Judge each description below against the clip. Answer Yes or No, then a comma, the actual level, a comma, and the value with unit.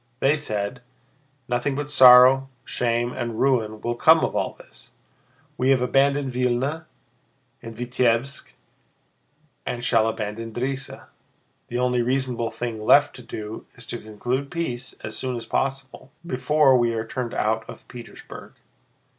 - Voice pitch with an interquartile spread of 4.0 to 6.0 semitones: No, narrow, 2.5 semitones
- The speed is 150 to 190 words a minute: No, average, 140 wpm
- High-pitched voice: No, low, 125 Hz